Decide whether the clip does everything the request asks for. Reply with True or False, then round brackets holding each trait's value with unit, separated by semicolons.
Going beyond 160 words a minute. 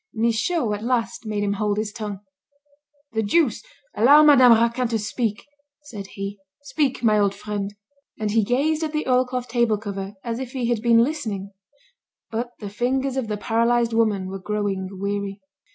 True (170 wpm)